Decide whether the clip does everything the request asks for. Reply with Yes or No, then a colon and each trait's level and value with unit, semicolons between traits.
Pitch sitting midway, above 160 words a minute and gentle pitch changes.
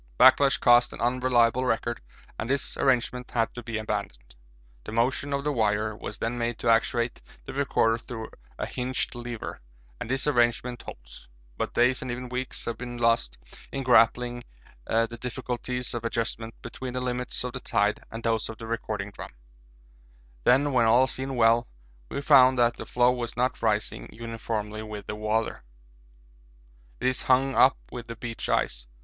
No: low, 120 Hz; average, 170 wpm; narrow, 1.9 semitones